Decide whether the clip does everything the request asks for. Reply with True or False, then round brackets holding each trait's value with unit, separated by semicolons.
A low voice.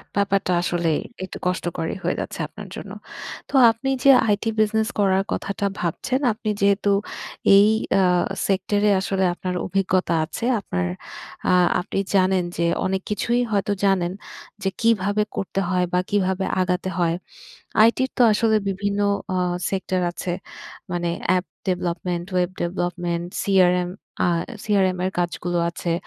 False (190 Hz)